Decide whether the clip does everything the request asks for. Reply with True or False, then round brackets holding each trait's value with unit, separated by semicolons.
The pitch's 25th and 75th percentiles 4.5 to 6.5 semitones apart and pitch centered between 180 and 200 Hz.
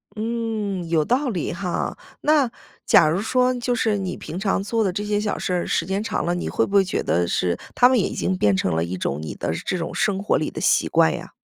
True (4.9 semitones; 195 Hz)